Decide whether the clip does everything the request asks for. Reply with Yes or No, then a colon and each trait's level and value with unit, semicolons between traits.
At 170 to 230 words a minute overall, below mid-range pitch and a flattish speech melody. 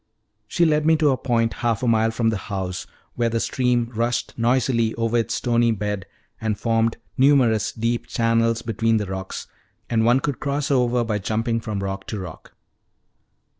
Yes: average, 175 wpm; low, 115 Hz; narrow, 1.8 semitones